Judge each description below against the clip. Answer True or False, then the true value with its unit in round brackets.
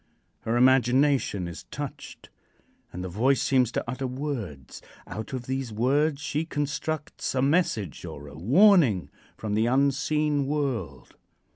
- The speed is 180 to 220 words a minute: False (135 wpm)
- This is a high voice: False (130 Hz)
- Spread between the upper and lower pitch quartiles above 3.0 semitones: True (4.7 semitones)